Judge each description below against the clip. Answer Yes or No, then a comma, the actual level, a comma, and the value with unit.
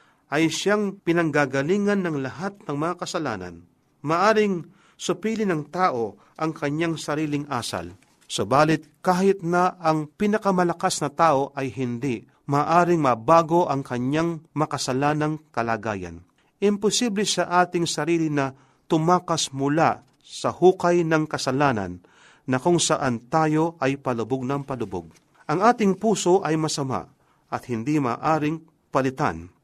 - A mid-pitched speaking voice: Yes, medium, 155 Hz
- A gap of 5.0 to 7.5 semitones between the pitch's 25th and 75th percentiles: No, average, 4.5 semitones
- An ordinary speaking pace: Yes, average, 120 wpm